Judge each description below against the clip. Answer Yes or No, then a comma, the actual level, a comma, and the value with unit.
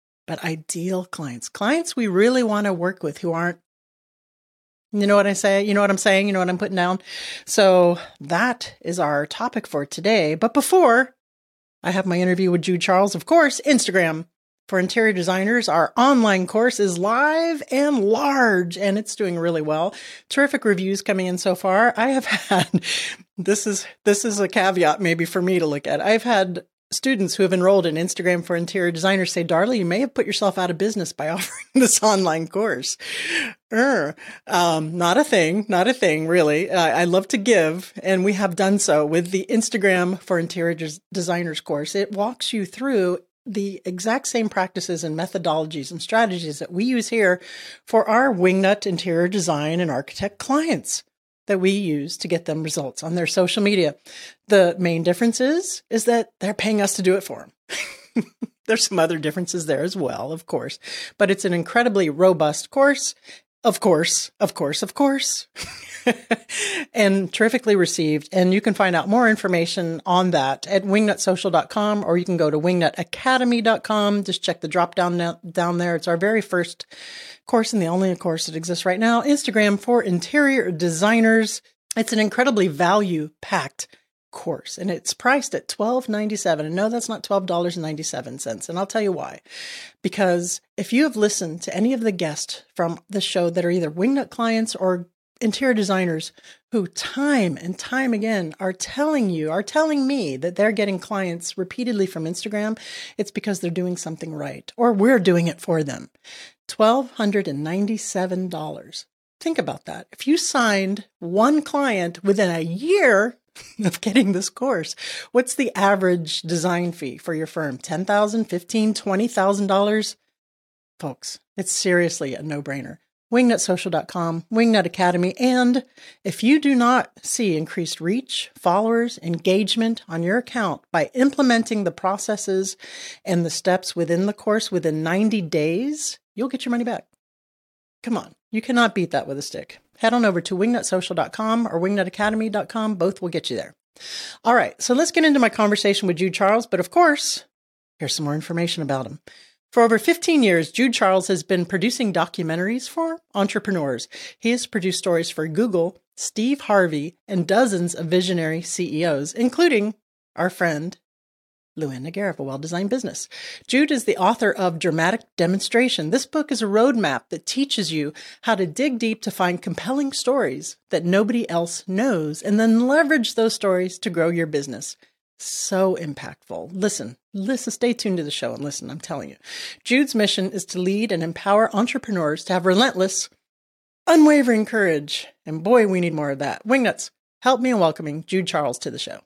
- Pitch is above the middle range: Yes, high, 195 Hz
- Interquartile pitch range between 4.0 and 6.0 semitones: Yes, average, 4.7 semitones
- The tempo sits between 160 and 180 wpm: Yes, average, 175 wpm